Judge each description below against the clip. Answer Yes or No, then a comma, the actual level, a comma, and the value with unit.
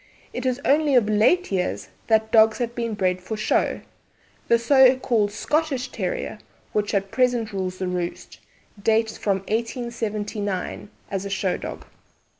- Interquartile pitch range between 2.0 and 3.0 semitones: No, average, 3.7 semitones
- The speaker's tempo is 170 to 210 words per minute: No, average, 150 wpm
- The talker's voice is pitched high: Yes, high, 220 Hz